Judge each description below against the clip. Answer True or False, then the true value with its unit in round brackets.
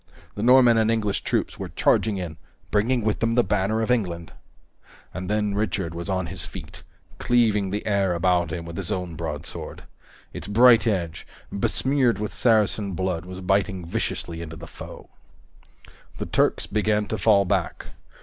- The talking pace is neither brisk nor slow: True (165 wpm)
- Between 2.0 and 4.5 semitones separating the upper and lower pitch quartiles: True (3.5 semitones)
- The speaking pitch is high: False (100 Hz)